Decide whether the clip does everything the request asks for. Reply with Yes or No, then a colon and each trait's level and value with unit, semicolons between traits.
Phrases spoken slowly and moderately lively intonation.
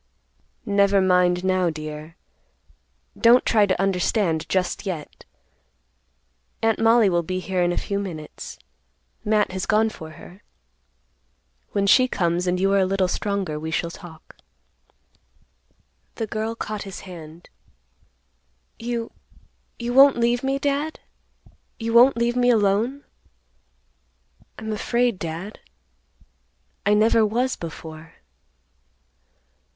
Yes: slow, 115 wpm; average, 4.4 semitones